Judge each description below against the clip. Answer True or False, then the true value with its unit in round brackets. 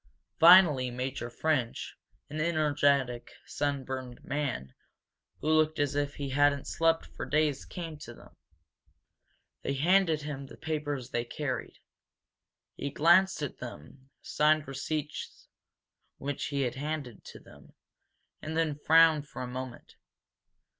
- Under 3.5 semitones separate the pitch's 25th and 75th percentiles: True (2.9 semitones)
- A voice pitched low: False (145 Hz)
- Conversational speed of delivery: False (125 wpm)